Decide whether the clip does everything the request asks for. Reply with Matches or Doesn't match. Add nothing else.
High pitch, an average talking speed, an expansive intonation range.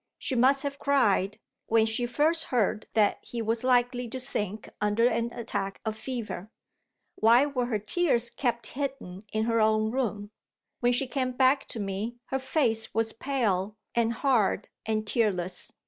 Doesn't match